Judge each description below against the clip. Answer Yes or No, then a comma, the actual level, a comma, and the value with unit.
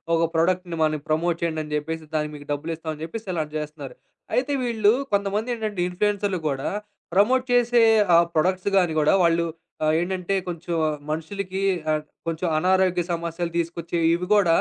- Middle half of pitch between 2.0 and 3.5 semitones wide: No, average, 3.9 semitones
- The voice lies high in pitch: No, medium, 170 Hz